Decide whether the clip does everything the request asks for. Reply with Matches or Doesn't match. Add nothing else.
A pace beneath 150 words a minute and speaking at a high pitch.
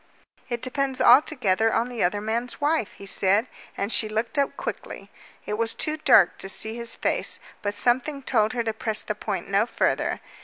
Doesn't match